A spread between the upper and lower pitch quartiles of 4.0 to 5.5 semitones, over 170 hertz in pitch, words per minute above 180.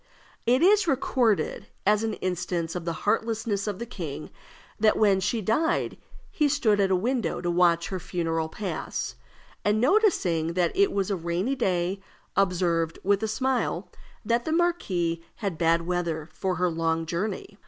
No: average, 4.9 semitones; high, 190 Hz; average, 165 wpm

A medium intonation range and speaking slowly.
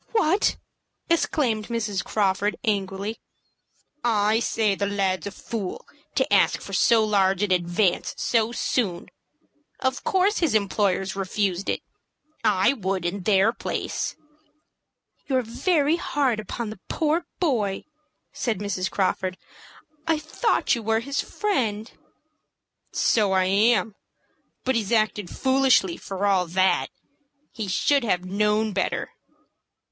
Yes: average, 3.9 semitones; slow, 125 wpm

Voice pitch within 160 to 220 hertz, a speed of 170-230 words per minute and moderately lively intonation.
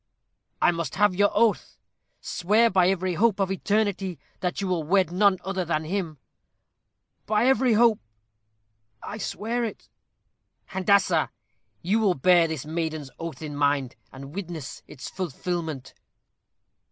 No: medium, 185 Hz; slow, 135 wpm; average, 4.1 semitones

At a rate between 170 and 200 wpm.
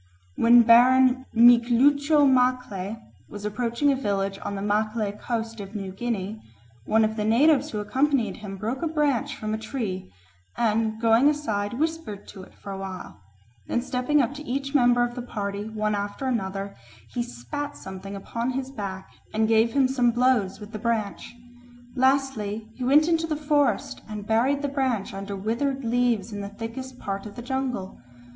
Yes: average, 175 wpm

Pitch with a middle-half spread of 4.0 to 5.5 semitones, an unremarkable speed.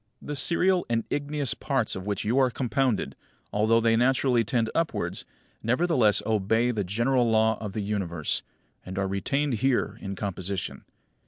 Yes: average, 4.4 semitones; average, 160 wpm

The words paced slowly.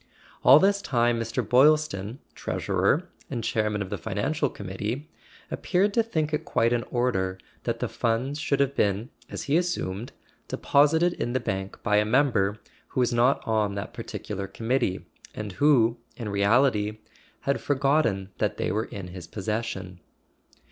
No: average, 160 wpm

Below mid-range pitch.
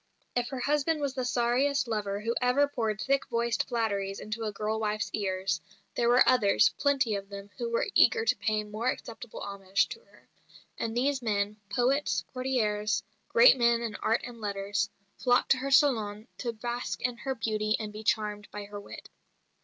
No: high, 230 Hz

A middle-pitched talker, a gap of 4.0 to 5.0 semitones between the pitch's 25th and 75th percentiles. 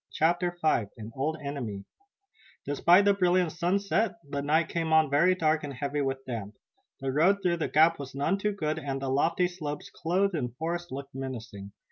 Yes: medium, 155 Hz; average, 4.4 semitones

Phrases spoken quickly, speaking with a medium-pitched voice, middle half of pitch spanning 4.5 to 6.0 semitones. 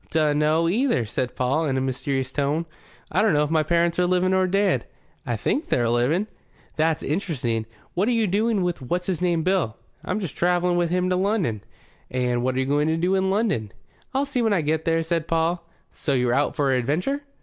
Yes: fast, 210 wpm; medium, 165 Hz; average, 5.1 semitones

